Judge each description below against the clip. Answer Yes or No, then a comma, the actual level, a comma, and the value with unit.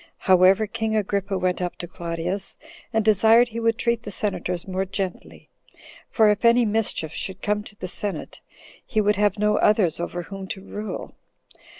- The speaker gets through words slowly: No, average, 175 wpm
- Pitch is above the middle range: Yes, high, 205 Hz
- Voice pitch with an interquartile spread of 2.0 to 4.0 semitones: Yes, average, 2.8 semitones